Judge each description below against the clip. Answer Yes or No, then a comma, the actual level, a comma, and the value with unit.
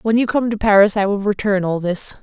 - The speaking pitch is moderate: No, high, 205 Hz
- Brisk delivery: Yes, fast, 270 wpm